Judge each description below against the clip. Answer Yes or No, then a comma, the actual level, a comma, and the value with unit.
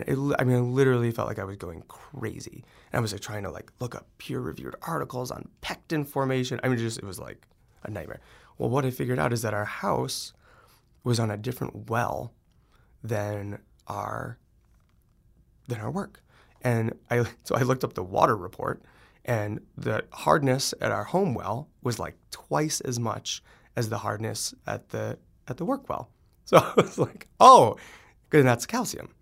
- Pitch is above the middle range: No, low, 120 Hz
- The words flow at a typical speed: Yes, average, 185 wpm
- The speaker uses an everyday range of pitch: Yes, average, 3.4 semitones